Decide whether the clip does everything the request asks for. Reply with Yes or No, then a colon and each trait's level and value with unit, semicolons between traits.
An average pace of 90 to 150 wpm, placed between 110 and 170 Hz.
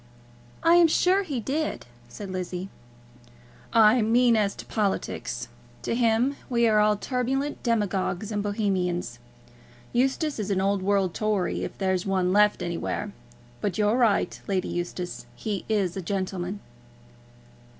No: average, 140 wpm; high, 205 Hz